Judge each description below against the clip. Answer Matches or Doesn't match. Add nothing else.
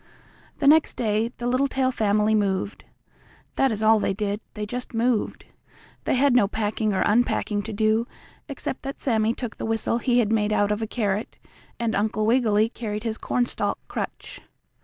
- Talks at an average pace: Matches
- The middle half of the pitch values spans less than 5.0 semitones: Matches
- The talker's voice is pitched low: Doesn't match